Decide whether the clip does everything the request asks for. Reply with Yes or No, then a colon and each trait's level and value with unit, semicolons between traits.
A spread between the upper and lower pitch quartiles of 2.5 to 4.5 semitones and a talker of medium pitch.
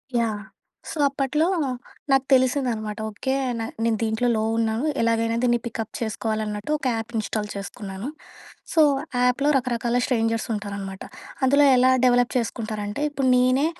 No: average, 2.8 semitones; high, 230 Hz